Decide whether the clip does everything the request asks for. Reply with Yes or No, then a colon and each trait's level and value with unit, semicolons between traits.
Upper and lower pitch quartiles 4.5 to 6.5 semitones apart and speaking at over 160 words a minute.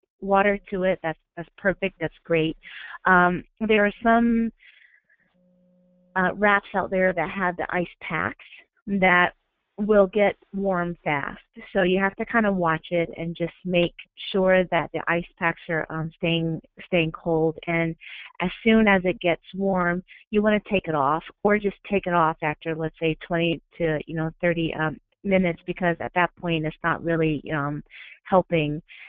No: average, 3.0 semitones; average, 175 wpm